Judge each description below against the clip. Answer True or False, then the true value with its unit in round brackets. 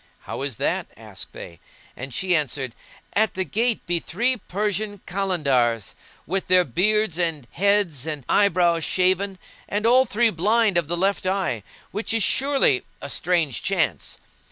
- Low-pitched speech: False (185 Hz)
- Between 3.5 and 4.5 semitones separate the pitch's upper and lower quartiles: False (5.0 semitones)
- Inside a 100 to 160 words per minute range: True (150 wpm)